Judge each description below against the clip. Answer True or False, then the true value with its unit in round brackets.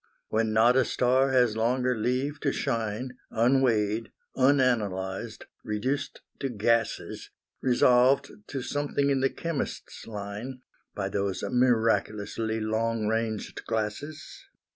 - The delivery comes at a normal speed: False (110 wpm)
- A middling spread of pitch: True (3.3 semitones)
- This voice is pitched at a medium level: False (115 Hz)